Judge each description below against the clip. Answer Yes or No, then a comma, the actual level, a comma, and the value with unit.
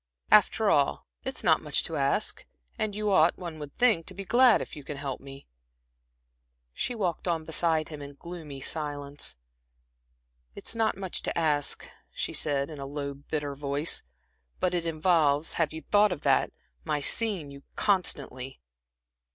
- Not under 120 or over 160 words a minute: No, average, 170 wpm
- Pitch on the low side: No, medium, 155 Hz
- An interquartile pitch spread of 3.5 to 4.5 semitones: Yes, average, 4.2 semitones